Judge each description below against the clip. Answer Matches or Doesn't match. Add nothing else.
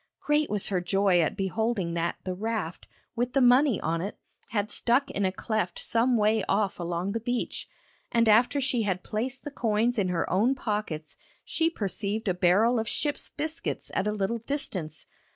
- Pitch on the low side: Doesn't match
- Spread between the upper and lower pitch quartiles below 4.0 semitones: Doesn't match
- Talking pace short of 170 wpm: Doesn't match